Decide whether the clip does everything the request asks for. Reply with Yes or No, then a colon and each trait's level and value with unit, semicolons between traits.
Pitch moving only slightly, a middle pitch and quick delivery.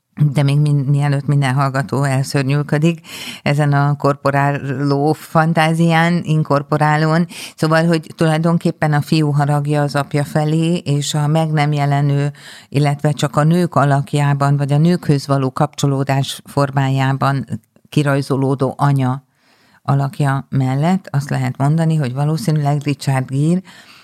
No: narrow, 1.9 semitones; medium, 145 Hz; average, 120 wpm